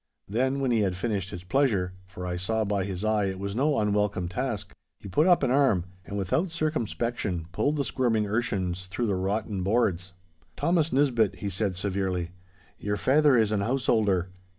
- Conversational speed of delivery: Yes, average, 175 wpm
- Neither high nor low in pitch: No, low, 105 Hz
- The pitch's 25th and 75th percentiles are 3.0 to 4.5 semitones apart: No, average, 5.0 semitones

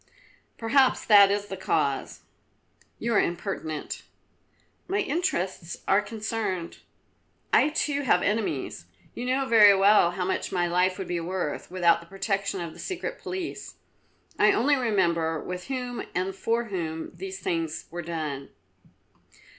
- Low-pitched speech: No, high, 195 Hz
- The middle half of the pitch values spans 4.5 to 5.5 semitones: Yes, average, 5.1 semitones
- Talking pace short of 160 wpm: Yes, average, 140 wpm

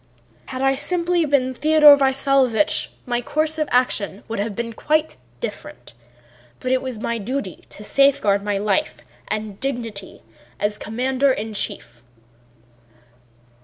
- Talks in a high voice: Yes, very high, 255 Hz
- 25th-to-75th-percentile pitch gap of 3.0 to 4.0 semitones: No, average, 4.6 semitones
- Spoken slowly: Yes, slow, 130 wpm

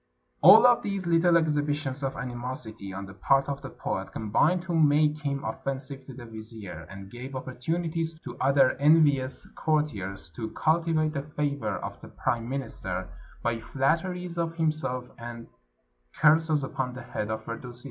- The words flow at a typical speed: Yes, average, 155 wpm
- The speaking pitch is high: No, low, 135 Hz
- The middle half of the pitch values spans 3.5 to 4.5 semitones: No, average, 4.9 semitones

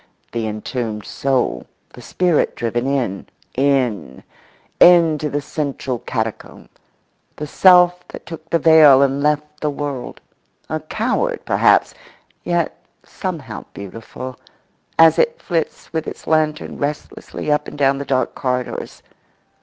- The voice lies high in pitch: No, medium, 140 Hz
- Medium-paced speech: No, slow, 125 wpm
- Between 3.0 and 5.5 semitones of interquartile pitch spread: Yes, average, 3.8 semitones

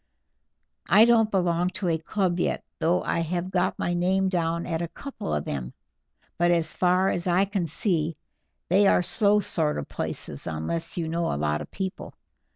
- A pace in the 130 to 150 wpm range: No, average, 185 wpm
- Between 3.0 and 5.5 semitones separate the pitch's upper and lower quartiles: No, narrow, 2.5 semitones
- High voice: No, medium, 175 Hz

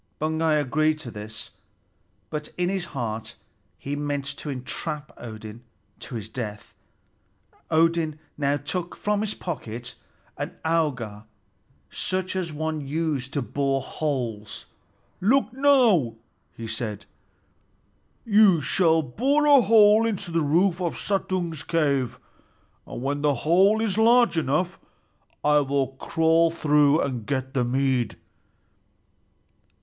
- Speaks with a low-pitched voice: No, medium, 150 Hz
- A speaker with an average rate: No, slow, 125 wpm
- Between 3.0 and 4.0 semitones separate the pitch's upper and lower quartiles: No, average, 5.3 semitones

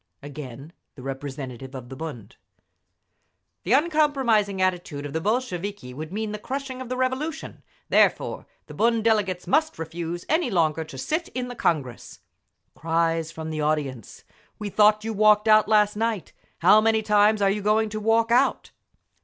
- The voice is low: No, high, 205 Hz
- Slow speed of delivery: No, average, 160 wpm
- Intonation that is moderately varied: No, wide, 6.1 semitones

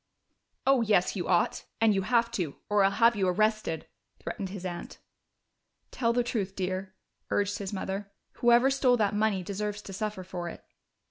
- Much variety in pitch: No, average, 3.1 semitones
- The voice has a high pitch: Yes, high, 205 Hz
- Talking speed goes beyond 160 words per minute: Yes, average, 175 wpm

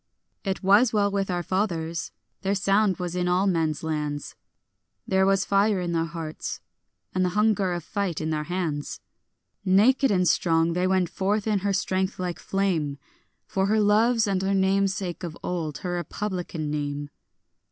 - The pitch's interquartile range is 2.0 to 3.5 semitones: Yes, average, 3.0 semitones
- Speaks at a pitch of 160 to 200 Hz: Yes, medium, 185 Hz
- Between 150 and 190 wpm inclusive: Yes, average, 170 wpm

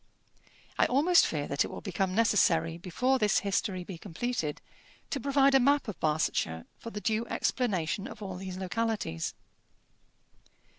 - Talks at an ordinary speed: Yes, average, 150 wpm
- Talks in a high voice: Yes, high, 200 Hz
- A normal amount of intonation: No, wide, 5.9 semitones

